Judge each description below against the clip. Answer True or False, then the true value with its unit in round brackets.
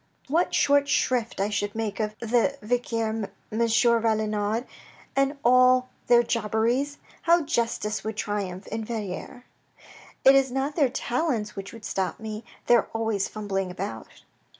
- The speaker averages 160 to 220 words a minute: False (145 wpm)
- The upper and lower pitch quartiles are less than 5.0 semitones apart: True (3.1 semitones)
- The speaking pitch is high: True (225 Hz)